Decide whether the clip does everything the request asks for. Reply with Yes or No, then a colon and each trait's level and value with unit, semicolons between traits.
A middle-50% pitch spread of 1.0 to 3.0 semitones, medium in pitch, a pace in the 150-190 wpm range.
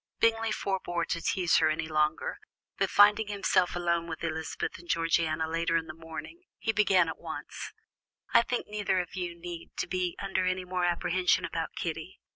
Yes: narrow, 2.6 semitones; medium, 175 Hz; average, 175 wpm